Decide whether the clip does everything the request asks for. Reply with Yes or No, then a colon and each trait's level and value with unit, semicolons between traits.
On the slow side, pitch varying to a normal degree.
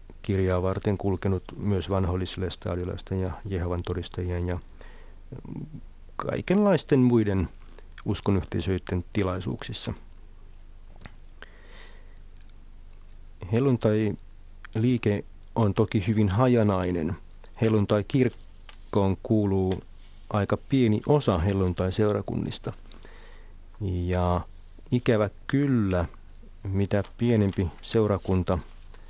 Yes: slow, 70 wpm; average, 4.8 semitones